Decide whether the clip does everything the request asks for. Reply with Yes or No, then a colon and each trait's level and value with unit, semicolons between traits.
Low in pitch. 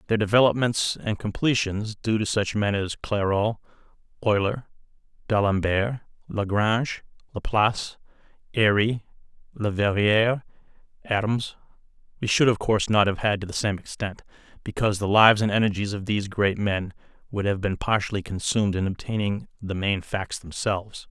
Yes: low, 105 Hz